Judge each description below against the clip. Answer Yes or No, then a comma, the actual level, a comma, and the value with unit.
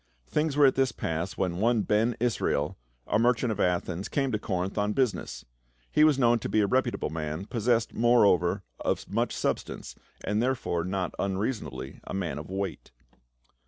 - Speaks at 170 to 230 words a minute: Yes, average, 180 wpm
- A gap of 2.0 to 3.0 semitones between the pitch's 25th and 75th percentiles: No, average, 5.2 semitones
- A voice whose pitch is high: No, low, 105 Hz